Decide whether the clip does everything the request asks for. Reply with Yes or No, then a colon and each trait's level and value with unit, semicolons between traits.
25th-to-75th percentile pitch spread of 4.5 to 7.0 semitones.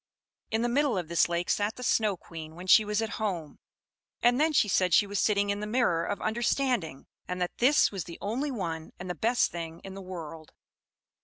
Yes: average, 5.0 semitones